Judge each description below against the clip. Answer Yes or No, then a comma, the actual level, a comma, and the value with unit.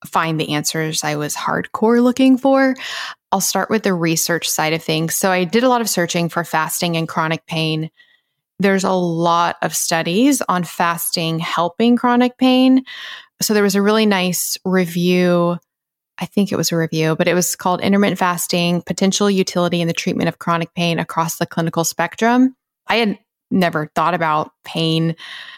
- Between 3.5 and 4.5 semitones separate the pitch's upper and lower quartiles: Yes, average, 3.8 semitones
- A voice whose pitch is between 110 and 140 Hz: No, medium, 175 Hz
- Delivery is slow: No, average, 175 wpm